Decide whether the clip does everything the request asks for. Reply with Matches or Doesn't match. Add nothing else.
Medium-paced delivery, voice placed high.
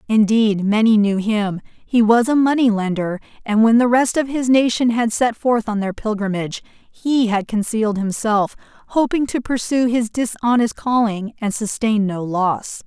Matches